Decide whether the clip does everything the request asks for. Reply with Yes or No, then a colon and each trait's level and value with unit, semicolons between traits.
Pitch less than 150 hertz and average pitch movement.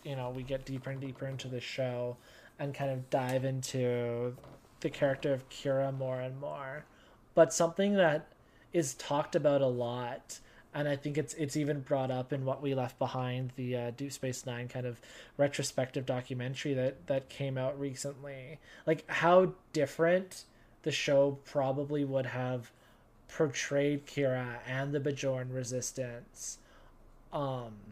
No: low, 135 Hz; narrow, 2.2 semitones